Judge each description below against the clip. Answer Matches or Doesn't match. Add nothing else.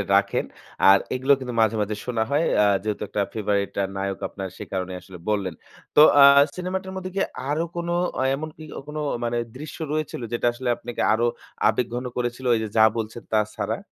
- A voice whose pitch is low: Matches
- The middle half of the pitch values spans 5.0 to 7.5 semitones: Matches